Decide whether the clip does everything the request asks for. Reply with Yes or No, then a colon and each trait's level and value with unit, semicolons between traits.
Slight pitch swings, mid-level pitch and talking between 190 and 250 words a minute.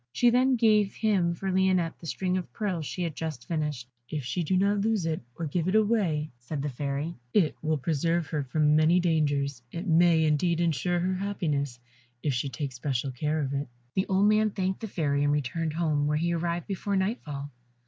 No: average, 4.3 semitones; medium, 165 Hz; fast, 205 wpm